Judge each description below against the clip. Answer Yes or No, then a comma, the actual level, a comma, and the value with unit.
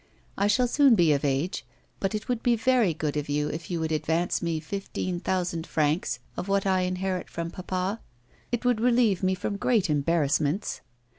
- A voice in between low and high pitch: Yes, medium, 180 Hz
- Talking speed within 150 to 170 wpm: No, average, 190 wpm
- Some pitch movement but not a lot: Yes, average, 4.4 semitones